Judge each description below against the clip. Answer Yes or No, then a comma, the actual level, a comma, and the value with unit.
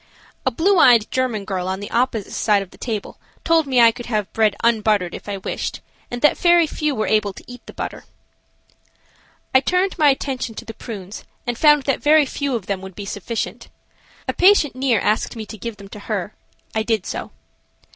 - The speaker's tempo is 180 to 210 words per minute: Yes, fast, 205 wpm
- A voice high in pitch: Yes, high, 230 Hz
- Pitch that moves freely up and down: No, average, 4.8 semitones